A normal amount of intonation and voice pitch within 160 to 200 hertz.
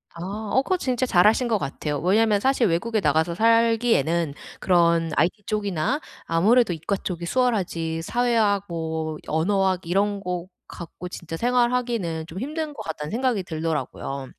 No: wide, 5.8 semitones; high, 190 Hz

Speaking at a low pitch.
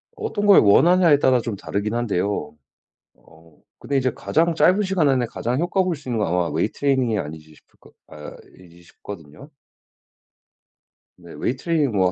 Yes: low, 120 Hz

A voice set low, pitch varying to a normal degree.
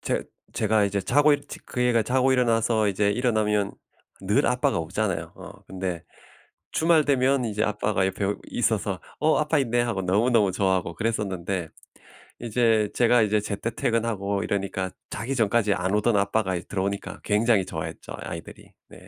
Yes: low, 105 Hz; average, 3.3 semitones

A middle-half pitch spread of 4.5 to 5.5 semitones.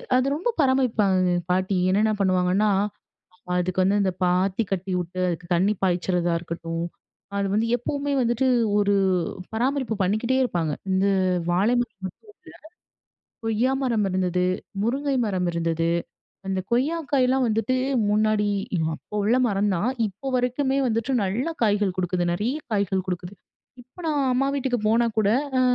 Yes: average, 5.0 semitones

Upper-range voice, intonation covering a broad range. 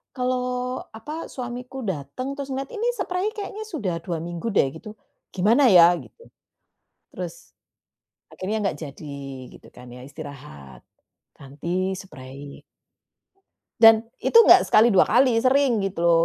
Yes: high, 210 Hz; wide, 7.7 semitones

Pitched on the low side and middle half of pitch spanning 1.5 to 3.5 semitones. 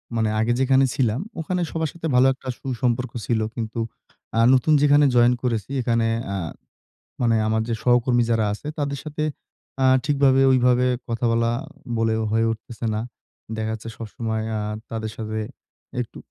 Yes: low, 120 Hz; average, 2.9 semitones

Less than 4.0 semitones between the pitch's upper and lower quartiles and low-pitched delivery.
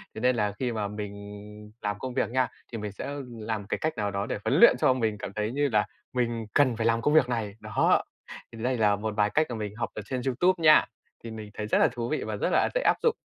Yes: average, 3.3 semitones; low, 115 Hz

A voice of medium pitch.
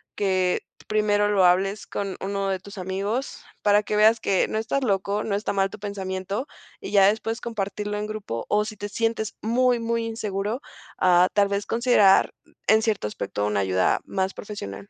No: high, 205 Hz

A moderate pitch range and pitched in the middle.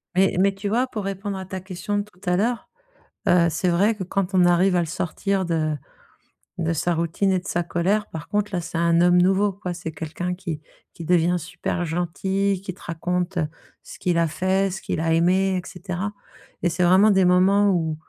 No: narrow, 2.3 semitones; medium, 180 Hz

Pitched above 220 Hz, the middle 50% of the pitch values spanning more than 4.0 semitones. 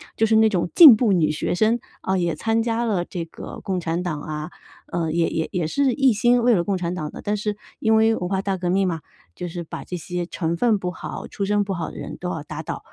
No: medium, 185 Hz; average, 4.4 semitones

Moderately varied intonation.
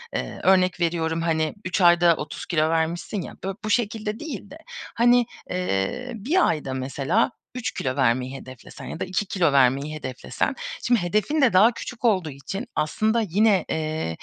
No: wide, 5.9 semitones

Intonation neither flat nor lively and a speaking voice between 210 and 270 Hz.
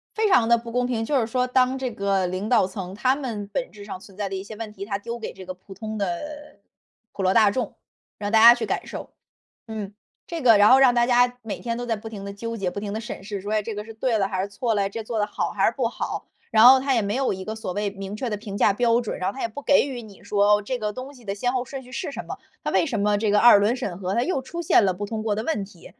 Yes: average, 3.5 semitones; high, 220 Hz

